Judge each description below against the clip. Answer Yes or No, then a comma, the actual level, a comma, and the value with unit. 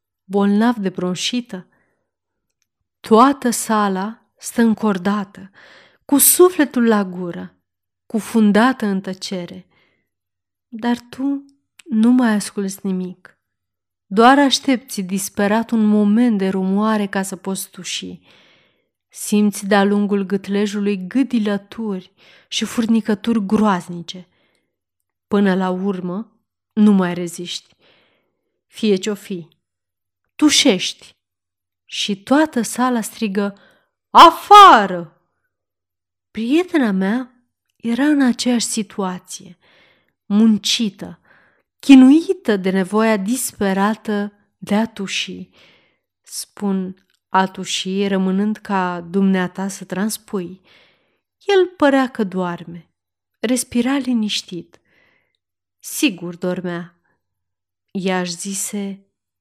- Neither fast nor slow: No, slow, 85 wpm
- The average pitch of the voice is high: Yes, high, 200 Hz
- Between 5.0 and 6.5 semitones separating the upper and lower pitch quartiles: No, average, 3.8 semitones